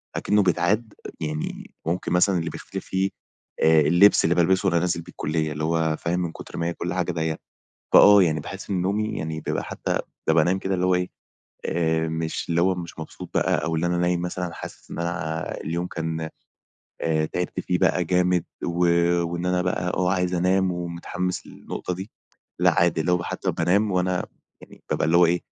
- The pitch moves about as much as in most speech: No, narrow, 1.9 semitones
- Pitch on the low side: Yes, very low, 85 Hz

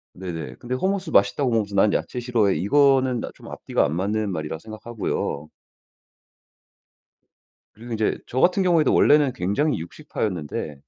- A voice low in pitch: Yes, low, 110 Hz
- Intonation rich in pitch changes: Yes, wide, 5.7 semitones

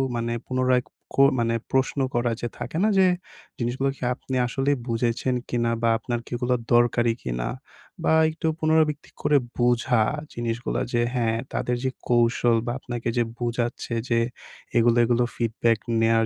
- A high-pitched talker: No, low, 120 Hz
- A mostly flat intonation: Yes, narrow, 1.7 semitones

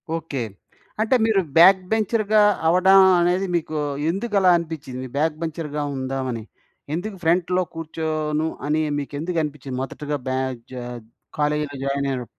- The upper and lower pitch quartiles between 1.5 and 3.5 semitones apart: No, average, 4.4 semitones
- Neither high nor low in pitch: Yes, medium, 155 Hz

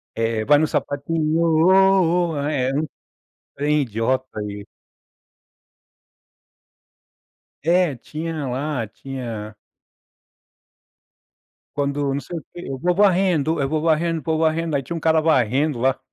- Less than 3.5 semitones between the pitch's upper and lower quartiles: No, average, 3.8 semitones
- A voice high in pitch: No, medium, 150 Hz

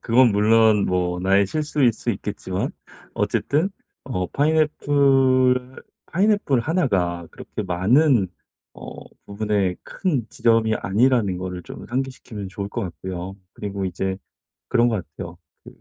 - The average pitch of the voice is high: No, low, 110 Hz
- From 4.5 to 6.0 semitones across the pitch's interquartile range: Yes, wide, 5.6 semitones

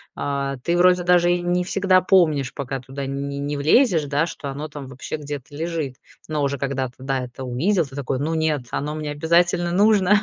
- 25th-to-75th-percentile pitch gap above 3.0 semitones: Yes, average, 4.0 semitones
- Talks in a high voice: No, medium, 150 Hz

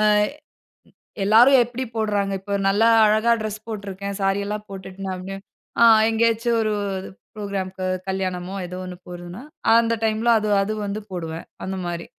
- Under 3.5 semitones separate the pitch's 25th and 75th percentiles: Yes, narrow, 2.5 semitones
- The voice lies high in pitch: Yes, high, 200 Hz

